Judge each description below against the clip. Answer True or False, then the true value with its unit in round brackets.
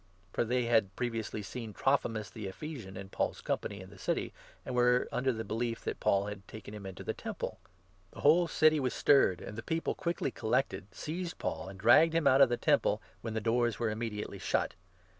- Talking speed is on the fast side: True (215 wpm)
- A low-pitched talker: True (115 Hz)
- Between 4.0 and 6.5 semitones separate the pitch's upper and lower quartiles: True (4.5 semitones)